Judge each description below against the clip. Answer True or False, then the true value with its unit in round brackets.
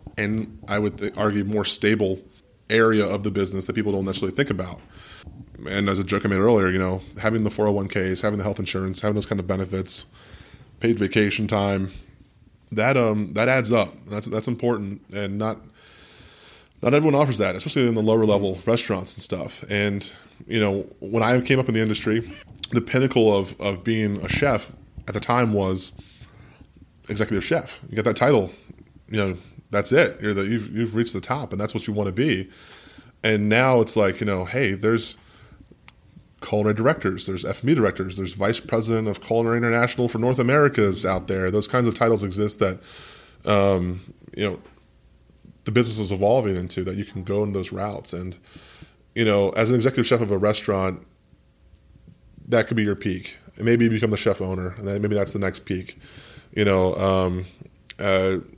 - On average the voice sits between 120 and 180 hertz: False (105 Hz)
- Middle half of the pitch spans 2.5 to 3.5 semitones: True (2.9 semitones)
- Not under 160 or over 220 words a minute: True (190 wpm)